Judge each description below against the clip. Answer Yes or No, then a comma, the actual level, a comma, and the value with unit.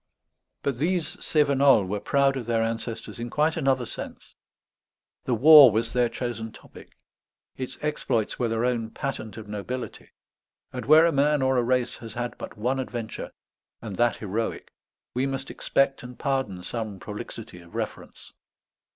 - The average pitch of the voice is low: Yes, low, 120 Hz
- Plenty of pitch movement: No, average, 3.3 semitones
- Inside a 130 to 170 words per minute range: Yes, average, 160 wpm